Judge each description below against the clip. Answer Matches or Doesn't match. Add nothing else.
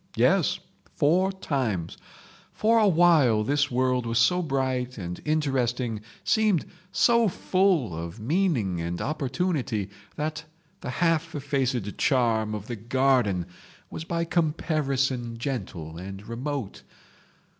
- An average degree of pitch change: Doesn't match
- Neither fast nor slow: Doesn't match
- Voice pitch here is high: Doesn't match